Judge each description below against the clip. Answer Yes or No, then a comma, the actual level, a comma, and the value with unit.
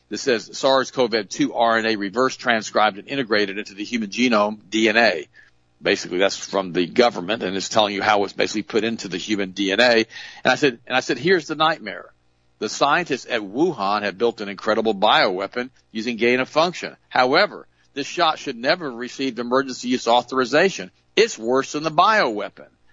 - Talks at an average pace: Yes, average, 175 wpm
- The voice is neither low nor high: No, low, 115 Hz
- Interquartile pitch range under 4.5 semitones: Yes, average, 4.1 semitones